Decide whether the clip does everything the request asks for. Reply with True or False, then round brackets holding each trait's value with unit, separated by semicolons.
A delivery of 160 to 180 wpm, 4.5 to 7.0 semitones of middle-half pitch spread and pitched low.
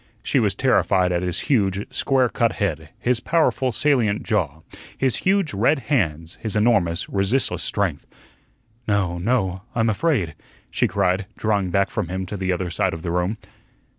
True (165 wpm; 4.9 semitones; 100 Hz)